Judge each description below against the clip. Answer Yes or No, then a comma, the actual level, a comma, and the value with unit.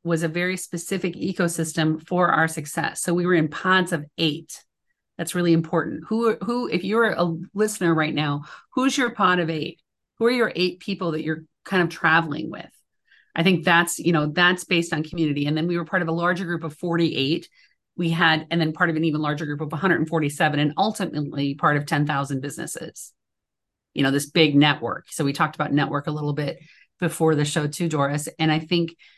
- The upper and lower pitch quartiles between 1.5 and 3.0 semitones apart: Yes, narrow, 2.4 semitones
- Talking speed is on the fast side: Yes, fast, 210 wpm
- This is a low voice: No, medium, 165 Hz